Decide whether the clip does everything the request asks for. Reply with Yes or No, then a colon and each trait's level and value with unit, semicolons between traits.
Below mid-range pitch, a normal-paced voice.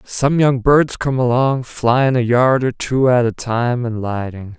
Yes: low, 125 Hz; average, 195 wpm